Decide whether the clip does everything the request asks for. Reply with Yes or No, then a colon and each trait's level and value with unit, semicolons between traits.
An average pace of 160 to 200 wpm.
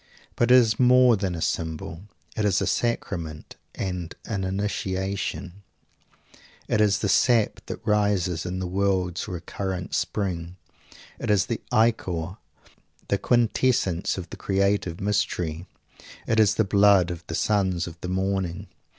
No: average, 140 wpm